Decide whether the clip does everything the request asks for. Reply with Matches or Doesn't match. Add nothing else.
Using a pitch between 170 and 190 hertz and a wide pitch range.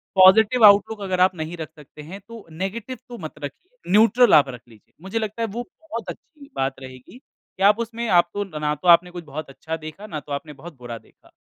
Matches